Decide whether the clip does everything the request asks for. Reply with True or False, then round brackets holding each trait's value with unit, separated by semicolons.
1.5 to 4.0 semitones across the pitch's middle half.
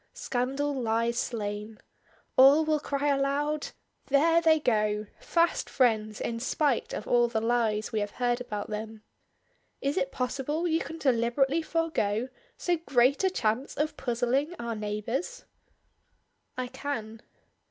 False (4.6 semitones)